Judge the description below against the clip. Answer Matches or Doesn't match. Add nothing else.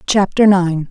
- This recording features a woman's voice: Matches